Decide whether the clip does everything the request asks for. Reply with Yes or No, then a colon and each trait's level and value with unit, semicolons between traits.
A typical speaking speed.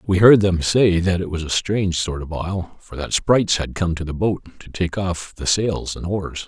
No: fast, 250 wpm